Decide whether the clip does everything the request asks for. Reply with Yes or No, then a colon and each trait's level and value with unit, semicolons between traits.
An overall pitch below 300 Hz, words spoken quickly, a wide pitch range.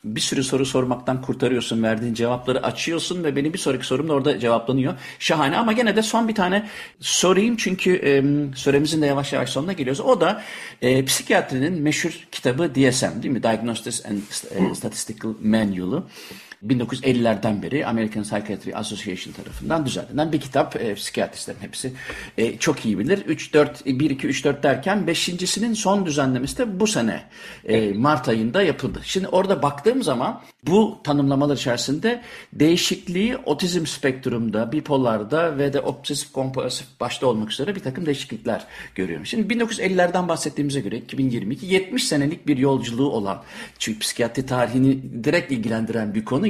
Yes: medium, 140 Hz; fast, 145 wpm; wide, 6.0 semitones